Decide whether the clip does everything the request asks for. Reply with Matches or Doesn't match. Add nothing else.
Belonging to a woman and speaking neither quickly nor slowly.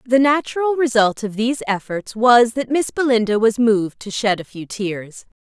Matches